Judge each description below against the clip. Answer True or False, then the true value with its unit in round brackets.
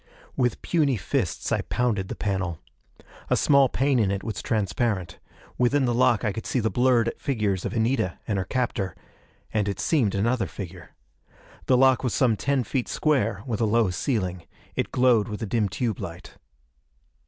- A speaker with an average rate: True (180 wpm)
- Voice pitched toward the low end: True (115 Hz)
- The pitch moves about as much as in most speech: True (4.2 semitones)